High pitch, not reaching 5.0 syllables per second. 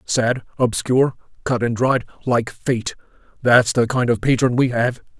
No: low, 120 Hz; 4.5 syllables/s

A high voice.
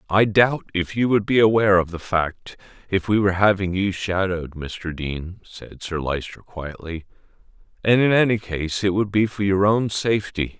No: very low, 95 Hz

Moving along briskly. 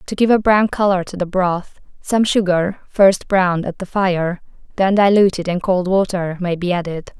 No: average, 190 wpm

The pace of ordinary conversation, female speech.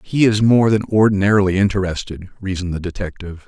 No: average, 155 wpm; male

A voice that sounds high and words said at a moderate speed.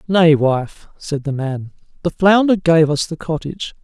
No: medium, 160 Hz; average, 170 wpm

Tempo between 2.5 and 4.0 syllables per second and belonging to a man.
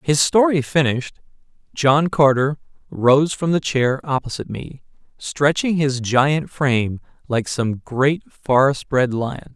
Yes: 3.9 syllables/s; male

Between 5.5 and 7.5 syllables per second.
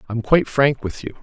Yes: 6.1 syllables/s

